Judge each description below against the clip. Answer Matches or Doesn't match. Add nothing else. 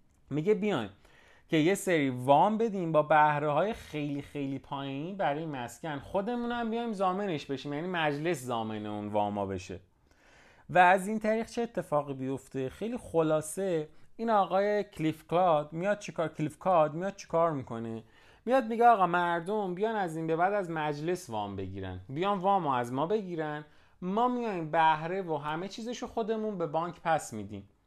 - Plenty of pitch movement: Matches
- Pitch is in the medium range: Matches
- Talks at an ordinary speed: Doesn't match